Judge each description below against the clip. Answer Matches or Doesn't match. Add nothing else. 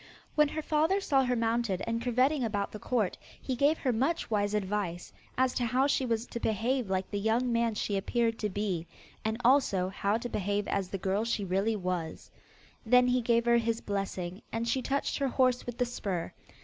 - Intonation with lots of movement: Doesn't match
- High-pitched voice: Matches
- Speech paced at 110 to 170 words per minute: Doesn't match